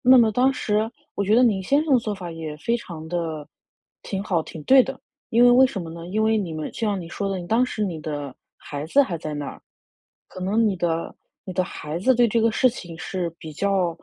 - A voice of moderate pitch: No, high, 195 Hz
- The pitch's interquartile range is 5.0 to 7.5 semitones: Yes, wide, 5.6 semitones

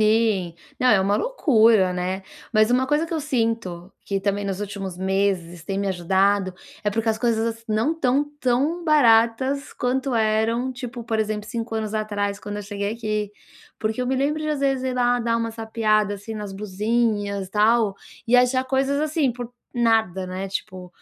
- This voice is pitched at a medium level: No, high, 220 Hz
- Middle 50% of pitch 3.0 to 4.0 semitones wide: Yes, average, 3.7 semitones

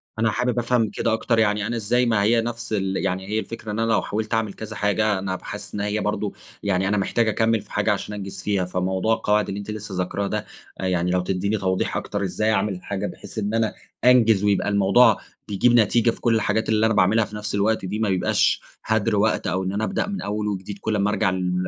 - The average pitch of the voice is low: Yes, low, 105 Hz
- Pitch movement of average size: No, narrow, 2.2 semitones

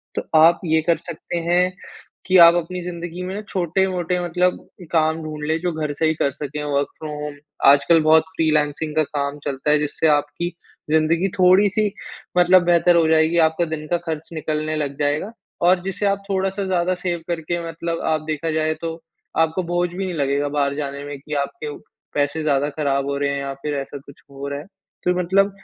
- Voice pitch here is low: No, medium, 160 Hz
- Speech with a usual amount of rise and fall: Yes, average, 3.0 semitones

